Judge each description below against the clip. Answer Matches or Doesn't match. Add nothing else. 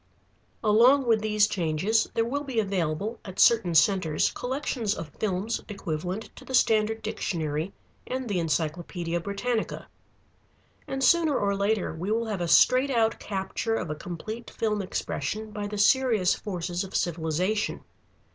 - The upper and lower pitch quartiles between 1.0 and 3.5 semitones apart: Doesn't match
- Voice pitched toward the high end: Matches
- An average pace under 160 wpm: Matches